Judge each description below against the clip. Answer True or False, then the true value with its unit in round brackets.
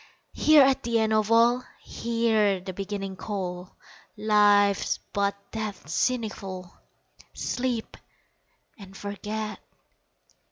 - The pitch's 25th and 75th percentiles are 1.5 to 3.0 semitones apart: True (2.6 semitones)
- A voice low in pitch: False (210 Hz)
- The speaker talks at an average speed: False (95 wpm)